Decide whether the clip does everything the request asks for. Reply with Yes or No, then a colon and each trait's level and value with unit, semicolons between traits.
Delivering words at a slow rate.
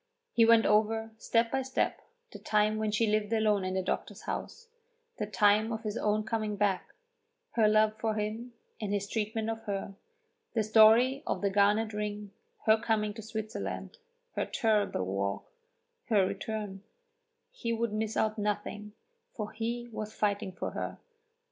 No: average, 160 wpm